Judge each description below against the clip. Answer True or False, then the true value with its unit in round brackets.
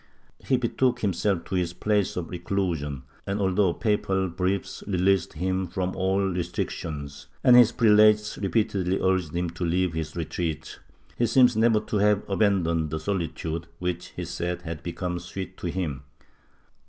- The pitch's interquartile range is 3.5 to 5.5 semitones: False (3.1 semitones)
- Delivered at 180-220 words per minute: False (155 wpm)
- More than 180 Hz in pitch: False (90 Hz)